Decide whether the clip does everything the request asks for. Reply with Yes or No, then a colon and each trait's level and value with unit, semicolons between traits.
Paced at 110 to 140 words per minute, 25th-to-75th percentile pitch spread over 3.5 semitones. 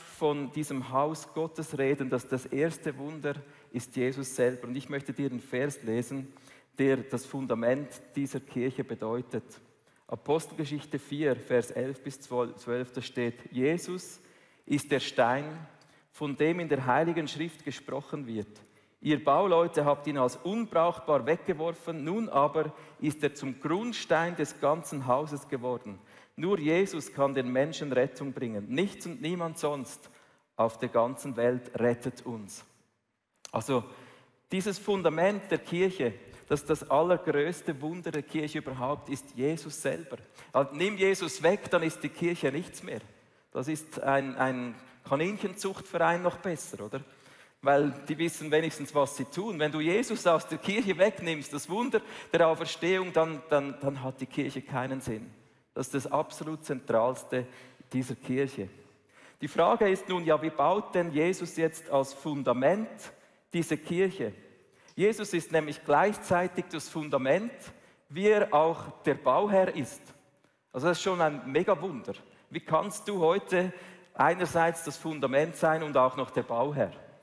No: average, 150 wpm; average, 3.9 semitones